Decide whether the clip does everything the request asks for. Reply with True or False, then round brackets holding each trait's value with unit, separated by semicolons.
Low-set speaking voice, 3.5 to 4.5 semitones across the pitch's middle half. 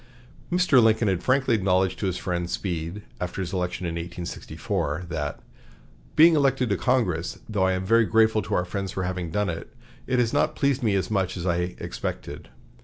True (95 Hz; 4.2 semitones)